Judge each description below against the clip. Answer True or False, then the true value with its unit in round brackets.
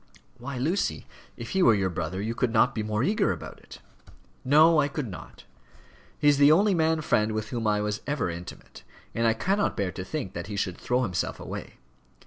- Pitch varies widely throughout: True (6.2 semitones)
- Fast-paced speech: True (210 wpm)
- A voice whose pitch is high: False (115 Hz)